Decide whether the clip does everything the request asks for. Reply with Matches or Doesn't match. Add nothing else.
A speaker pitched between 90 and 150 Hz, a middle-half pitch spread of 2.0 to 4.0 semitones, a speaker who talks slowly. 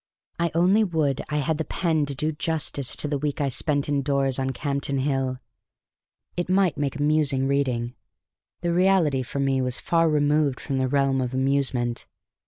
Doesn't match